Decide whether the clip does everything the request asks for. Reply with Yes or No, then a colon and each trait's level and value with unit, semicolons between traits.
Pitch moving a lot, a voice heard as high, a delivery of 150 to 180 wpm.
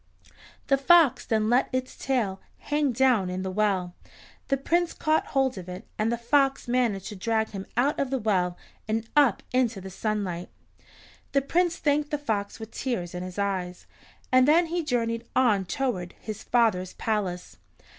Yes: wide, 5.7 semitones; high, 230 Hz; average, 175 wpm